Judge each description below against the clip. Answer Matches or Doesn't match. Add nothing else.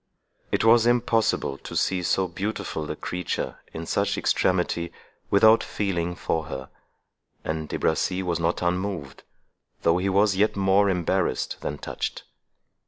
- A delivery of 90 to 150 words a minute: Matches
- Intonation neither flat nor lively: Matches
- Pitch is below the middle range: Matches